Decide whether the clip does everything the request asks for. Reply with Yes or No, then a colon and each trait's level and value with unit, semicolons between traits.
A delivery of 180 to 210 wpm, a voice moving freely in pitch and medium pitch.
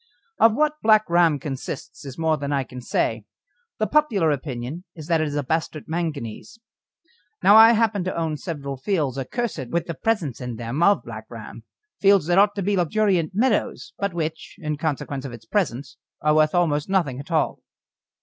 Yes: average, 190 wpm; wide, 5.8 semitones; medium, 160 Hz